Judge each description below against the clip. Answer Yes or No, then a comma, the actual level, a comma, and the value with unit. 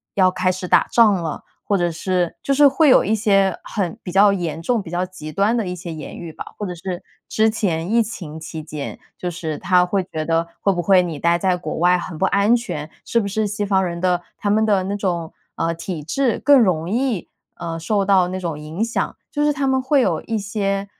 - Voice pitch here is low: No, medium, 185 Hz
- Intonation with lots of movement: No, average, 3.7 semitones